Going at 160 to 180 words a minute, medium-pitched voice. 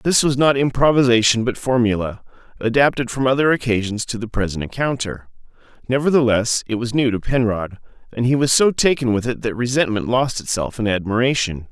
No: average, 170 wpm; low, 120 Hz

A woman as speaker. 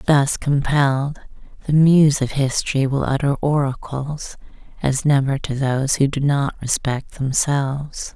Yes: female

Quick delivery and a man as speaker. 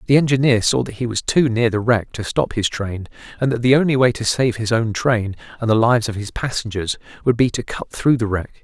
Yes: fast, 255 wpm; male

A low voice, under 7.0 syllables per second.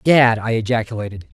Yes: low, 115 Hz; 5.8 syllables/s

